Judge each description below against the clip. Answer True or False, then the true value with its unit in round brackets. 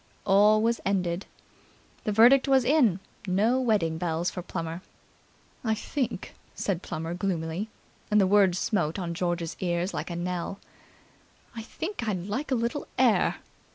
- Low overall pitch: False (195 Hz)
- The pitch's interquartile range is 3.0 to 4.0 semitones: False (4.6 semitones)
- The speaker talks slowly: False (150 wpm)